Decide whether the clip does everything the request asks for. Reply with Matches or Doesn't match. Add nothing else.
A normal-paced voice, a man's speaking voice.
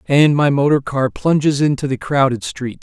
Matches